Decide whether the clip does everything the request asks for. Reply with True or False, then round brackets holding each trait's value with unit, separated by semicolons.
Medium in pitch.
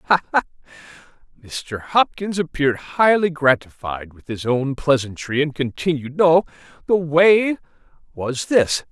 True (150 Hz)